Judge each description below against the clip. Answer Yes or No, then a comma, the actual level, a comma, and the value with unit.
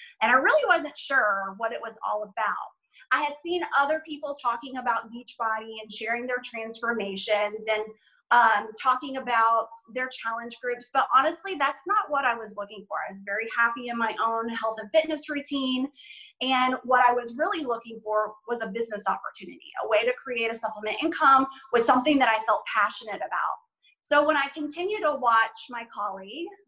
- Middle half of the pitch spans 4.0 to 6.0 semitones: Yes, average, 4.5 semitones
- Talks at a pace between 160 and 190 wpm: Yes, average, 185 wpm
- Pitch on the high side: Yes, high, 240 Hz